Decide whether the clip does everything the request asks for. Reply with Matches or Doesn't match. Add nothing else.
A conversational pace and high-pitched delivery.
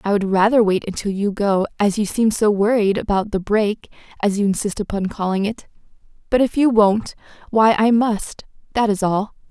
Matches